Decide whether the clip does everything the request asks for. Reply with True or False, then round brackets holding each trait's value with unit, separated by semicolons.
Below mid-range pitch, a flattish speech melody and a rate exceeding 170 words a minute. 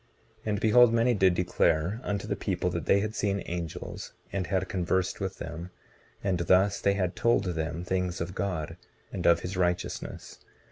True (95 Hz; 2.3 semitones; 180 wpm)